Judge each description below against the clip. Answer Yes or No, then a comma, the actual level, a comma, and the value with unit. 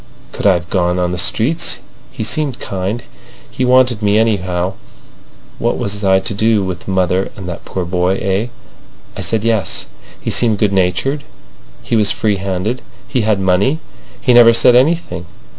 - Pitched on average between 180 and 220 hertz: No, low, 100 Hz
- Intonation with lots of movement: No, average, 4.1 semitones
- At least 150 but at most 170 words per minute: Yes, average, 160 wpm